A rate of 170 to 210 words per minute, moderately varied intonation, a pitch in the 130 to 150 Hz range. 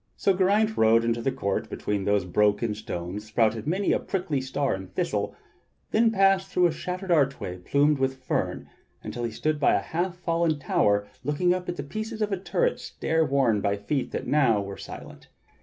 No: average, 190 wpm; wide, 8.9 semitones; medium, 140 Hz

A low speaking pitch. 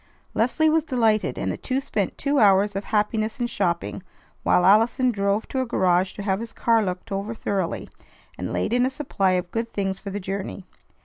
No: high, 210 Hz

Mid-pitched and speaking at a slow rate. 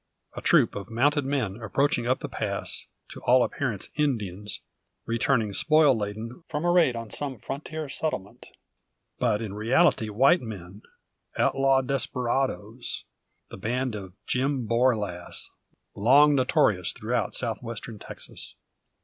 No: low, 120 Hz; slow, 130 wpm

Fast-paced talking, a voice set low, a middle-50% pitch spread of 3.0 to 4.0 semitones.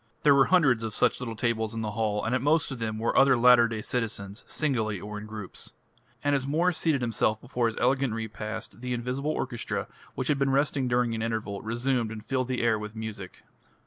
Yes: fast, 215 wpm; low, 120 Hz; average, 3.3 semitones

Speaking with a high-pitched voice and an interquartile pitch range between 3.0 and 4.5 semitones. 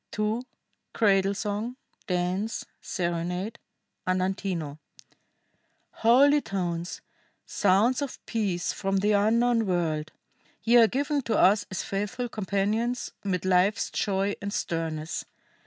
Yes: high, 200 Hz; average, 3.7 semitones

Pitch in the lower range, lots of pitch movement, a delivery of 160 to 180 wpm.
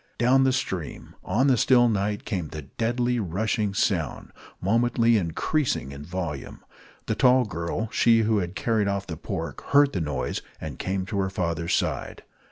Yes: low, 100 Hz; wide, 5.7 semitones; average, 170 wpm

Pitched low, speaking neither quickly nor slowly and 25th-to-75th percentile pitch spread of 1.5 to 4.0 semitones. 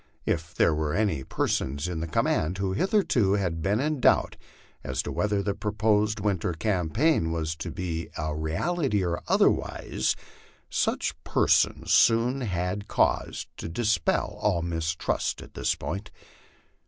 No: very low, 95 Hz; average, 145 wpm; average, 4.5 semitones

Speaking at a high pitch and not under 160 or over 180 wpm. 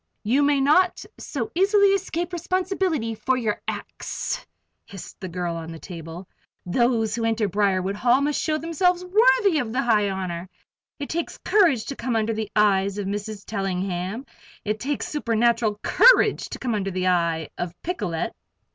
Yes: high, 225 Hz; average, 165 wpm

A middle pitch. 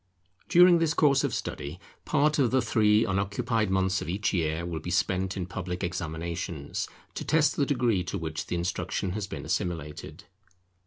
No: very low, 95 Hz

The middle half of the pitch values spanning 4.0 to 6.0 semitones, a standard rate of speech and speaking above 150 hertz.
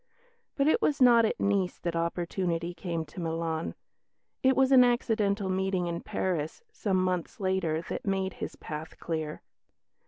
No: average, 3.6 semitones; average, 155 wpm; medium, 185 Hz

